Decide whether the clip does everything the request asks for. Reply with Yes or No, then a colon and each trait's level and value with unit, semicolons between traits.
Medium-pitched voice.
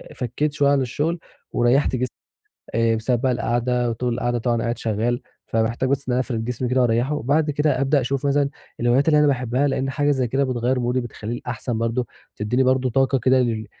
No: low, 125 Hz